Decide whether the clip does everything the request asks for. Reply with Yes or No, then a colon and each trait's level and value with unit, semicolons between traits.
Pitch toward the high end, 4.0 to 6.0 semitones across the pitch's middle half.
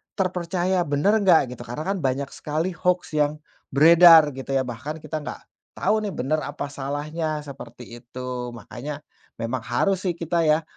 No: medium, 150 Hz; average, 4.4 semitones